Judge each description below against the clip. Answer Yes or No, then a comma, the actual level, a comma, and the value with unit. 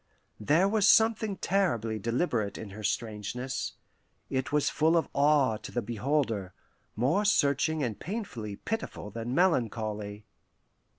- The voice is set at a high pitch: No, low, 125 Hz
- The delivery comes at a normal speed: No, slow, 125 wpm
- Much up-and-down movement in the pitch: Yes, wide, 7.4 semitones